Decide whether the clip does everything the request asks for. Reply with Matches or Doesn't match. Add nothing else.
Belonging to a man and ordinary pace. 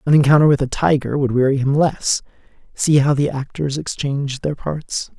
Matches